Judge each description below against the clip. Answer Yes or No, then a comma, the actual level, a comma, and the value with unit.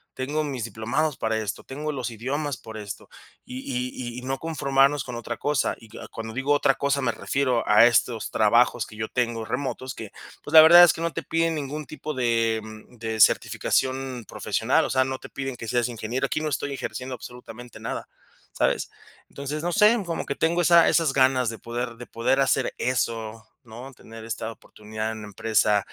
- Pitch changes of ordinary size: Yes, average, 3.7 semitones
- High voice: No, low, 125 Hz